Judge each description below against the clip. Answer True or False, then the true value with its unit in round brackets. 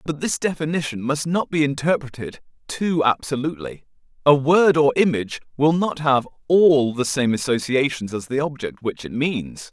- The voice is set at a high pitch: False (140 Hz)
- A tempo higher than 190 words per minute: False (160 wpm)